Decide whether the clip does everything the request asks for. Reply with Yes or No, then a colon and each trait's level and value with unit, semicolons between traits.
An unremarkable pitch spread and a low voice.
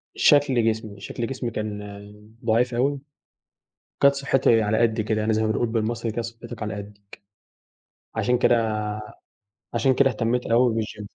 No: narrow, 2.2 semitones; low, 115 Hz